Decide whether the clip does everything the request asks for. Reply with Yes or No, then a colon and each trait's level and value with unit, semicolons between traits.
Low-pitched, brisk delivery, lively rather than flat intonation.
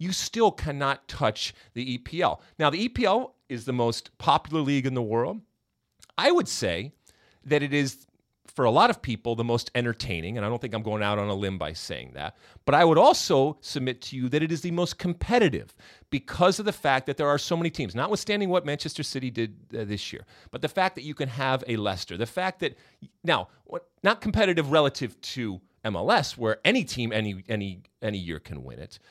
Yes: low, 125 Hz; fast, 210 wpm; wide, 5.7 semitones